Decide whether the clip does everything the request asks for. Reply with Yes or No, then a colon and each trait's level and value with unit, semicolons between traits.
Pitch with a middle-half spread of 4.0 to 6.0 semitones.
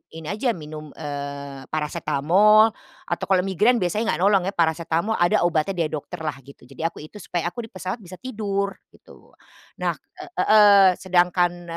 Yes: average, 4.5 semitones